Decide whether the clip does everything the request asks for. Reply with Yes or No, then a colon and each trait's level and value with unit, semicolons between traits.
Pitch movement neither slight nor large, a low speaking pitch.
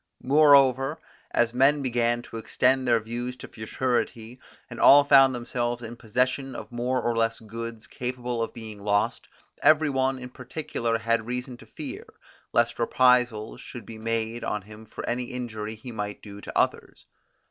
No: narrow, 2.2 semitones; low, 120 Hz